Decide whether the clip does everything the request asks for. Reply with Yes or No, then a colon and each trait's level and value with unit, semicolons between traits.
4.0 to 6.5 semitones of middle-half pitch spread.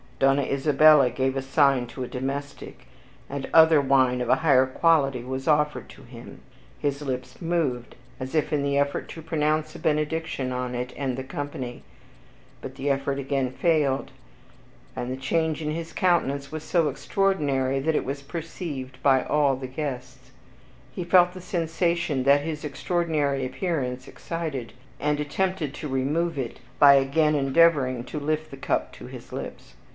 No: average, 3.1 semitones